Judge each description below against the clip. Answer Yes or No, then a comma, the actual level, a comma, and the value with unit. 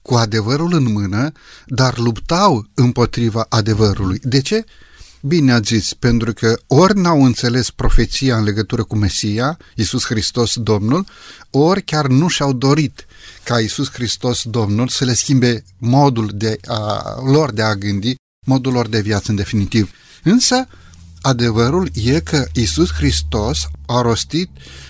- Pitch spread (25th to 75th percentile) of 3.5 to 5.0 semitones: Yes, average, 3.8 semitones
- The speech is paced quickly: No, average, 145 wpm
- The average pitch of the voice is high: No, low, 120 Hz